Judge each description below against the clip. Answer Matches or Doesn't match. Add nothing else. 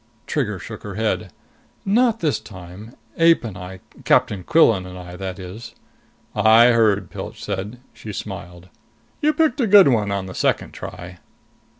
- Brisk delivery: Doesn't match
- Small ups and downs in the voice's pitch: Doesn't match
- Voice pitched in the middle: Doesn't match